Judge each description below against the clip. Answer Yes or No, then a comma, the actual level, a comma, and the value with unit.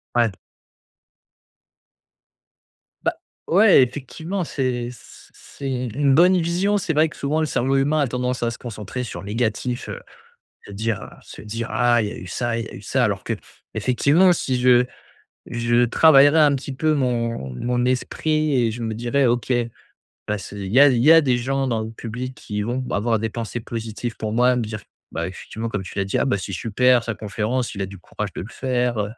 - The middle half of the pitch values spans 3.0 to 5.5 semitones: Yes, average, 3.4 semitones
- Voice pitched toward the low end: Yes, low, 120 Hz